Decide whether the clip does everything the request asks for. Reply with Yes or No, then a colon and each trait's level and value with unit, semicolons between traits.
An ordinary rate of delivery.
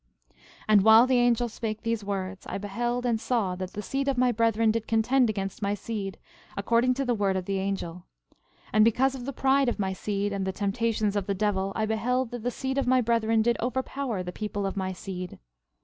No: fast, 225 wpm